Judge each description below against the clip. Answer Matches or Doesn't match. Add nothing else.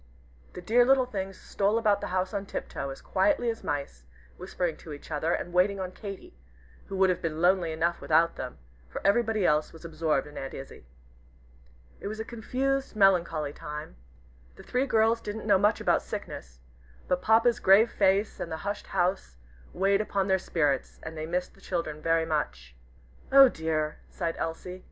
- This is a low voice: Doesn't match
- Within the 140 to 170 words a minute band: Doesn't match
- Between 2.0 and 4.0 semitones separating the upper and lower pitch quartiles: Doesn't match